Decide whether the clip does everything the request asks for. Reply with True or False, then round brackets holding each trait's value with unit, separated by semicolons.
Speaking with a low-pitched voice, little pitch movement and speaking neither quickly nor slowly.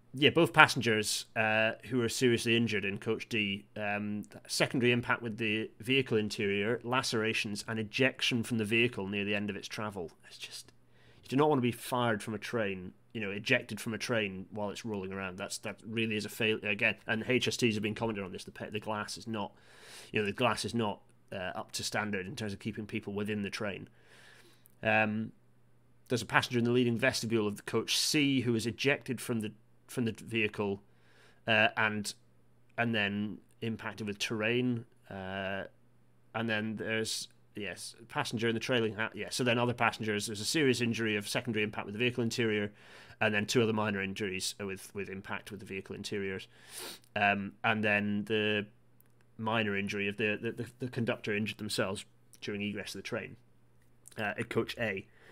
True (110 Hz; 2.2 semitones; 195 wpm)